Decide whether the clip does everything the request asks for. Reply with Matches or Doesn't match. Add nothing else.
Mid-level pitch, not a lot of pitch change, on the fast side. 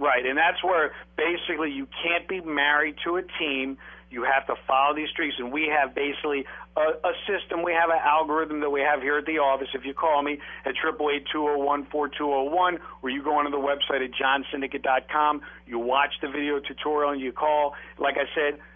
Matches